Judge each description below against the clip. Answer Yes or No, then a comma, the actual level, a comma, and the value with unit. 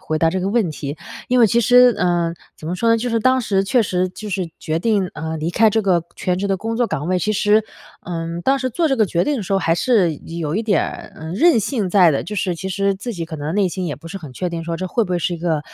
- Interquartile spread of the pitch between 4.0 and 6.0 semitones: Yes, average, 4.7 semitones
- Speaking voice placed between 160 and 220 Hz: Yes, medium, 185 Hz